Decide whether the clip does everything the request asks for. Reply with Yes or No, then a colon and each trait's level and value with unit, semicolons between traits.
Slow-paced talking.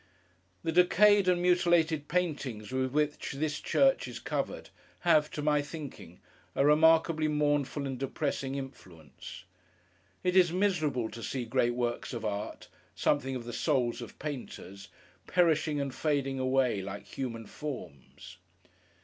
Yes: slow, 130 wpm